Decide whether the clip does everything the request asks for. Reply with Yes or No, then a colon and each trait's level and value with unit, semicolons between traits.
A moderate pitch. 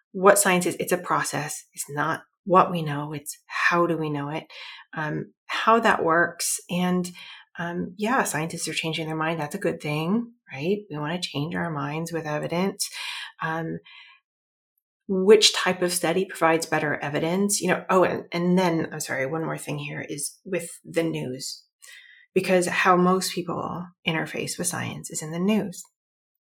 Yes: medium, 170 Hz